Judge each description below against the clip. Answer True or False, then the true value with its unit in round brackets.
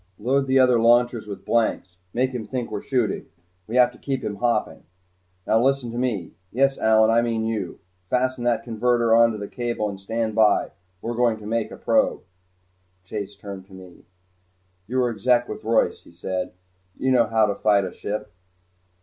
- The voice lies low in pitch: True (115 Hz)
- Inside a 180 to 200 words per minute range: True (190 wpm)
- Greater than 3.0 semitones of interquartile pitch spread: False (2.7 semitones)